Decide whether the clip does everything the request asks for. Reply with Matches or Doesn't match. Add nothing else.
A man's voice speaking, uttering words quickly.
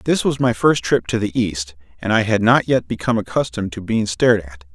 Matches